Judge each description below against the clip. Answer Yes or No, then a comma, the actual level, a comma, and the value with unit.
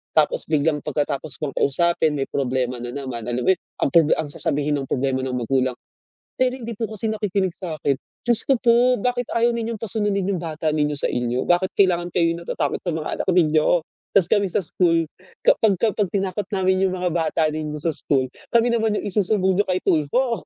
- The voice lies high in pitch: No, medium, 170 Hz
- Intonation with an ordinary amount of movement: No, wide, 6.0 semitones